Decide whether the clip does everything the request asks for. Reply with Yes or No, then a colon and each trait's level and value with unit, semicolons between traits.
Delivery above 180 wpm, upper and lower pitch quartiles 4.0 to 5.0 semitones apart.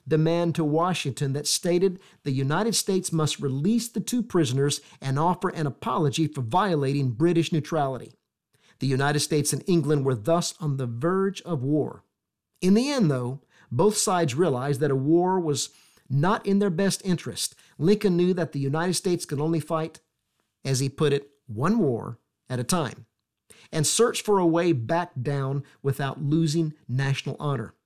No: average, 170 wpm; average, 4.3 semitones